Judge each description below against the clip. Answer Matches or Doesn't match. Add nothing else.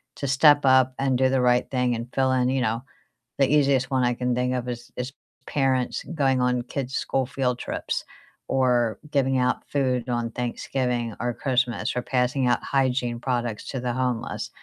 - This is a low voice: Matches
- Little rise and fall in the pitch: Matches